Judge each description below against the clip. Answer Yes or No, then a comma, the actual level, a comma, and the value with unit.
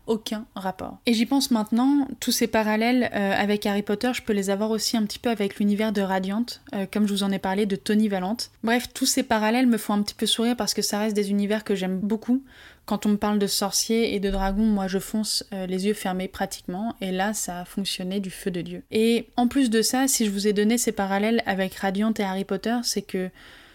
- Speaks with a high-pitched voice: Yes, high, 210 Hz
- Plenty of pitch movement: No, narrow, 2.6 semitones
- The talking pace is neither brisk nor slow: No, fast, 250 wpm